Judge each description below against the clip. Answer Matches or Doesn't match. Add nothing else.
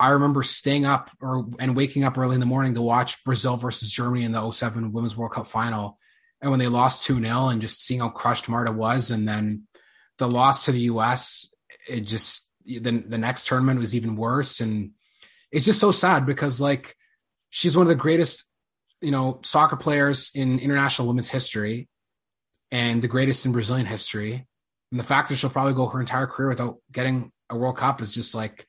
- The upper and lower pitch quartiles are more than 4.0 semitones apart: Doesn't match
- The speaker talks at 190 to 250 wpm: Matches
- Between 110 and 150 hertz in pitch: Matches